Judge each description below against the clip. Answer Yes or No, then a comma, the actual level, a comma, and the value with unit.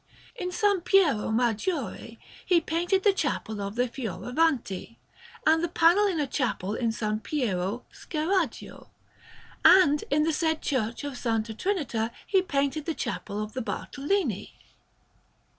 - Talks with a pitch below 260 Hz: No, very high, 285 Hz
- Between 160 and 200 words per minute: No, average, 140 wpm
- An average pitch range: No, wide, 6.9 semitones